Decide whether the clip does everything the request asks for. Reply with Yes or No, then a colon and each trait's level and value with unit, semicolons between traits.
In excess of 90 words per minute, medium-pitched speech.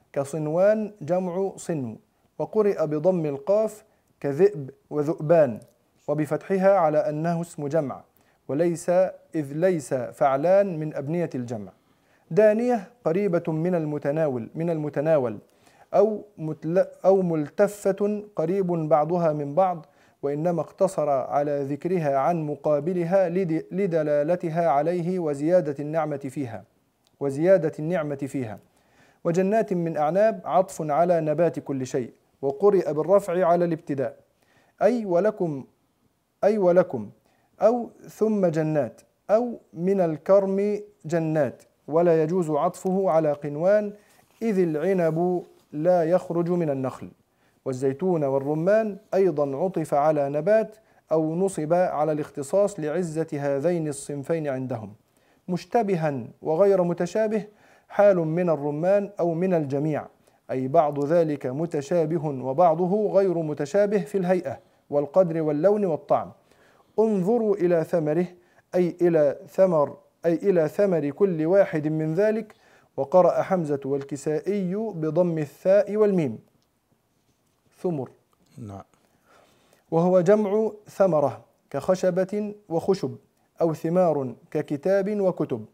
Yes: average, 105 wpm; medium, 170 Hz